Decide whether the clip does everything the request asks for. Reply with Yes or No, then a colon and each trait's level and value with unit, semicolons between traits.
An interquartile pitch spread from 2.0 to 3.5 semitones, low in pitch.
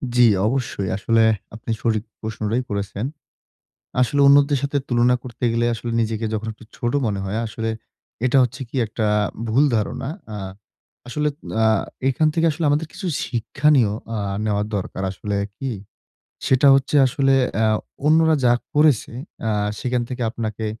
No: average, 3.9 semitones; low, 120 Hz